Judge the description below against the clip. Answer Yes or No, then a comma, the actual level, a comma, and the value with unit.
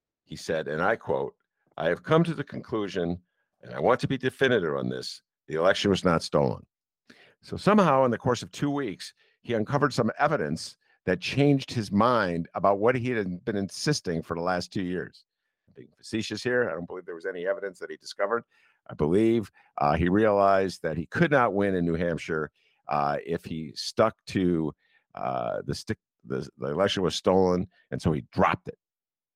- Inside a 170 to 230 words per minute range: Yes, average, 195 wpm